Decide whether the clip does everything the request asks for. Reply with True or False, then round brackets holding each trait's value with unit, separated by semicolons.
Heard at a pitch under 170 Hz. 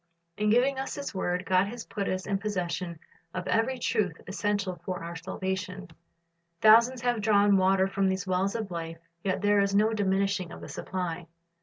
False (195 Hz)